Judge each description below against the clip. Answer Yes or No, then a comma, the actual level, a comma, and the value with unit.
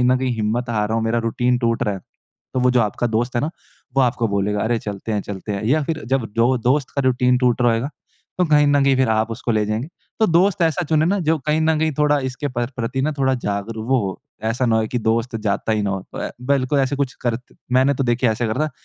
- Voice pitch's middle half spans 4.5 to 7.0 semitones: No, average, 3.8 semitones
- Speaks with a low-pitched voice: Yes, low, 125 Hz